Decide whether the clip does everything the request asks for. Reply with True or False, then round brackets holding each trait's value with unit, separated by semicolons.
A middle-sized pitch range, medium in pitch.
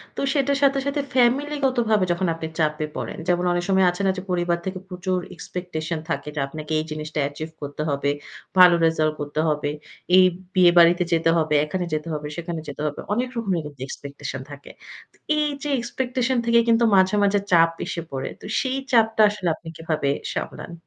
False (6.3 semitones; 175 Hz)